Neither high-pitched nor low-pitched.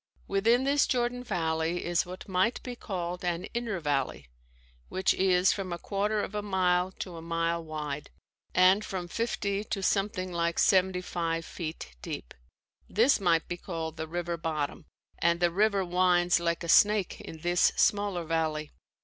Yes: medium, 180 Hz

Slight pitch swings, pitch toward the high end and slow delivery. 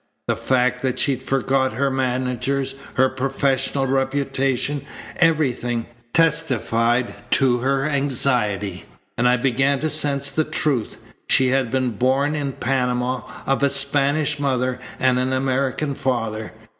No: narrow, 1.6 semitones; low, 135 Hz; slow, 130 wpm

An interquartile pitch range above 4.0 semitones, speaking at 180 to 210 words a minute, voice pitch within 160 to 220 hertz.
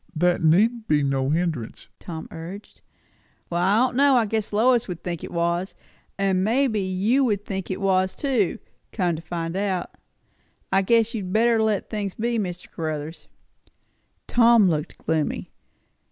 No: average, 4.5 semitones; average, 160 wpm; high, 190 Hz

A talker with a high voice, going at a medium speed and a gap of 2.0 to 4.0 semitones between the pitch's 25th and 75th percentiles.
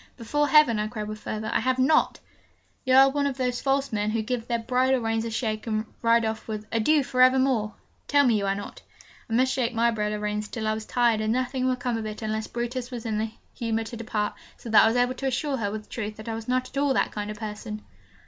No: high, 230 Hz; fast, 265 wpm; average, 2.9 semitones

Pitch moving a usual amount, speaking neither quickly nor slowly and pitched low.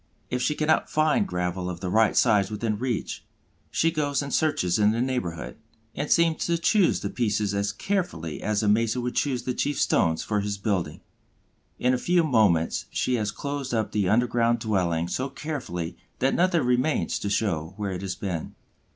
No: wide, 6.2 semitones; average, 185 wpm; low, 110 Hz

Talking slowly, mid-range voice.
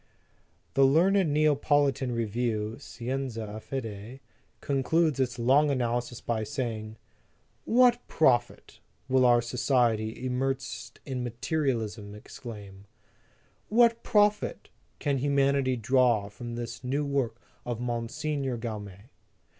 No: slow, 105 wpm; low, 125 Hz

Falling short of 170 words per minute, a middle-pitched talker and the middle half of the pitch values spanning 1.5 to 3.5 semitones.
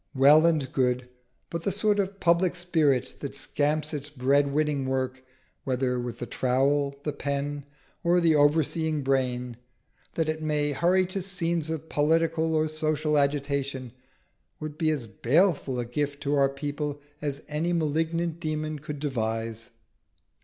Yes: average, 150 wpm; medium, 150 Hz; average, 2.9 semitones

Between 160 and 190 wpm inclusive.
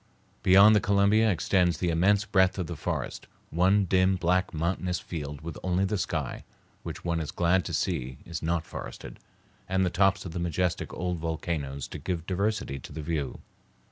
Yes: average, 180 wpm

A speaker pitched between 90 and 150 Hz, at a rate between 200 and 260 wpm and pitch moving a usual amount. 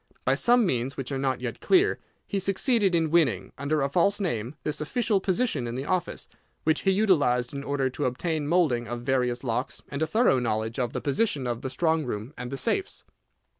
No: medium, 140 Hz; fast, 205 wpm; wide, 6.5 semitones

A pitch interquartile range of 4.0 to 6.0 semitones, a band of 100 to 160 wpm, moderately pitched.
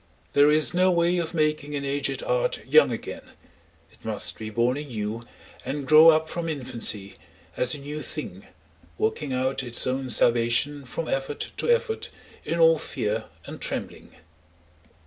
Yes: average, 4.4 semitones; average, 155 wpm; medium, 145 Hz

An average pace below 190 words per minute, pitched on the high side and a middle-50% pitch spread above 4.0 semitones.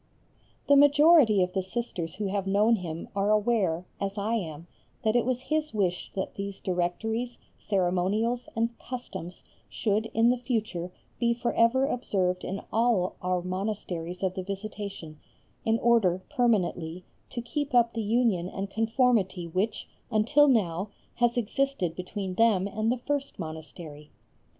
Yes: average, 150 wpm; high, 210 Hz; average, 4.5 semitones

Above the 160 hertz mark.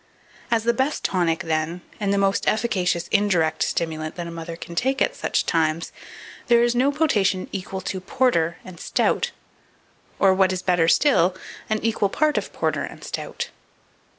Yes: high, 190 Hz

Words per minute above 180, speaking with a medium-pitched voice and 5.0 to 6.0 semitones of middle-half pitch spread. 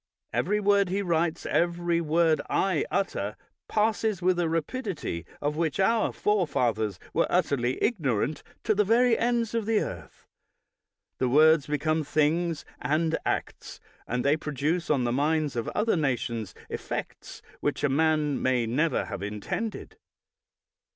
No: average, 140 wpm; medium, 160 Hz; wide, 5.6 semitones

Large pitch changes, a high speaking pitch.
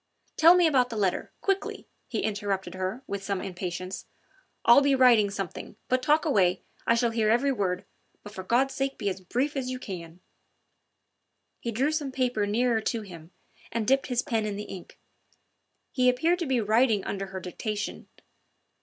No: average, 4.8 semitones; high, 225 Hz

